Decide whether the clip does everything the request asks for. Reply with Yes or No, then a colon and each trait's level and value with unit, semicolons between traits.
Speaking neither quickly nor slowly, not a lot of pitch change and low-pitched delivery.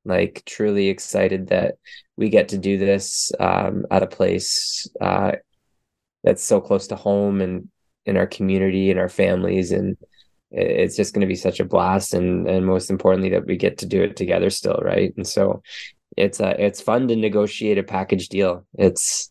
Yes: average, 185 wpm; narrow, 1.3 semitones; very low, 95 Hz